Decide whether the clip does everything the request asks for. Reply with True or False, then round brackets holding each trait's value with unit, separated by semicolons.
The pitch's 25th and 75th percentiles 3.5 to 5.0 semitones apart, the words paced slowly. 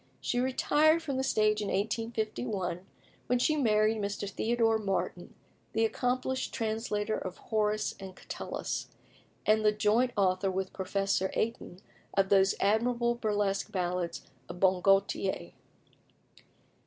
False (3.1 semitones; 125 wpm)